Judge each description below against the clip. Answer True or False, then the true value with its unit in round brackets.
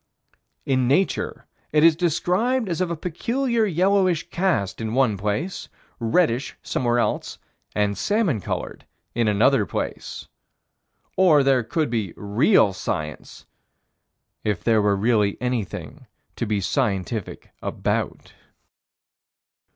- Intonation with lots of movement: True (8.9 semitones)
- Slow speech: True (115 wpm)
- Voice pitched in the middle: False (130 Hz)